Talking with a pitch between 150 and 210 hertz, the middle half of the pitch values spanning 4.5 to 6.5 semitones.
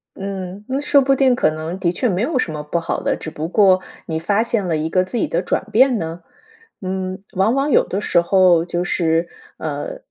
Yes: medium, 185 Hz; average, 5.1 semitones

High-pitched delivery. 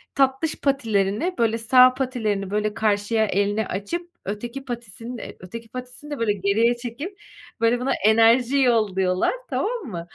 Yes: high, 230 Hz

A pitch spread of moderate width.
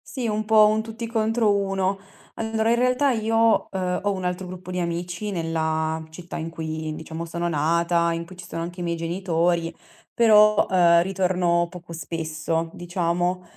Yes: average, 3.8 semitones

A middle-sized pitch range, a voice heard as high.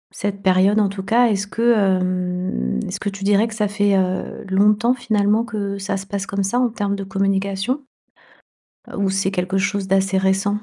No: narrow, 1.3 semitones; high, 200 Hz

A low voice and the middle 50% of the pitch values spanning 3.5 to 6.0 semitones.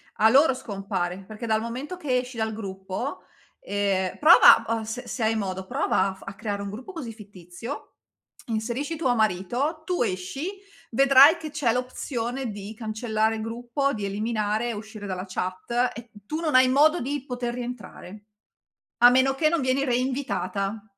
No: high, 230 Hz; average, 4.3 semitones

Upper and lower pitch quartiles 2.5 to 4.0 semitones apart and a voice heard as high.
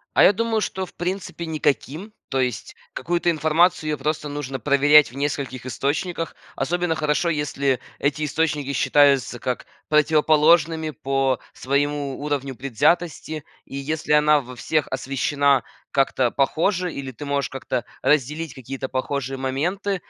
No: average, 2.9 semitones; medium, 145 Hz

